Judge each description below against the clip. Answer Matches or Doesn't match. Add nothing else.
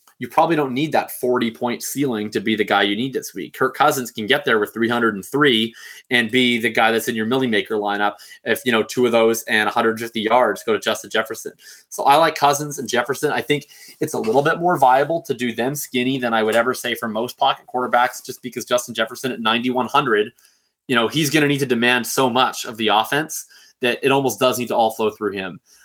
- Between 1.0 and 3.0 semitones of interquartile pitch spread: Matches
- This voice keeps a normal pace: Doesn't match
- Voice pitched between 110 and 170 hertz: Matches